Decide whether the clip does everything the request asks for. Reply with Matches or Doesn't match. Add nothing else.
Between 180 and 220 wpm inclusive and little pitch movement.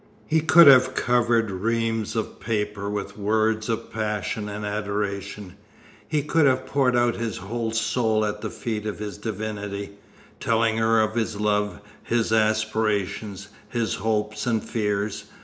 Doesn't match